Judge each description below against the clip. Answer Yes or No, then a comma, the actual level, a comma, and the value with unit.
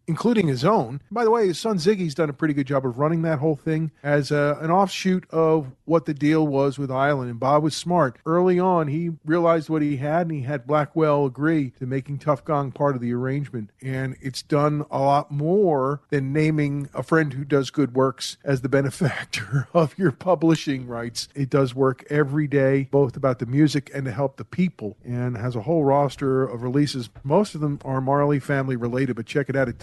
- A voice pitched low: No, medium, 145 Hz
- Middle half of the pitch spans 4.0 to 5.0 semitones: No, average, 3.0 semitones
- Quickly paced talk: Yes, fast, 215 wpm